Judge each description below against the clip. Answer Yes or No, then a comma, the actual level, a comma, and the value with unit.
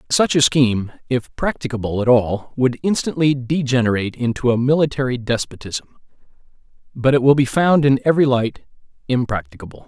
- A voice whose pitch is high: No, low, 130 Hz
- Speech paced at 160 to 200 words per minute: No, average, 140 wpm